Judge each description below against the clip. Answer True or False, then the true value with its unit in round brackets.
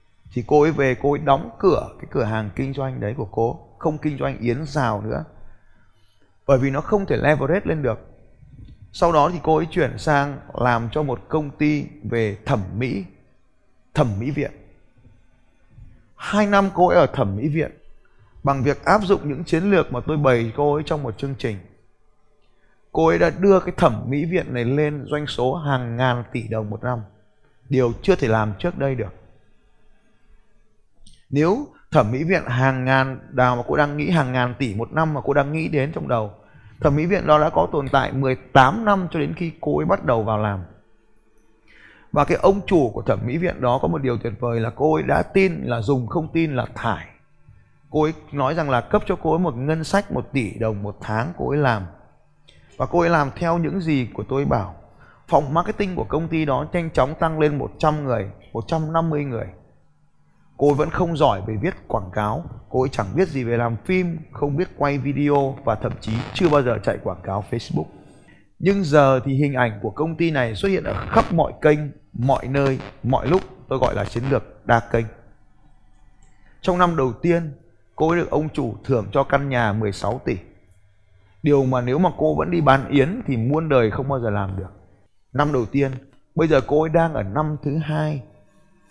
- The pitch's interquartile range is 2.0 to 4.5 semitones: False (5.1 semitones)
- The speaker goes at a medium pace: True (210 wpm)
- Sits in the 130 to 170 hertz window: True (135 Hz)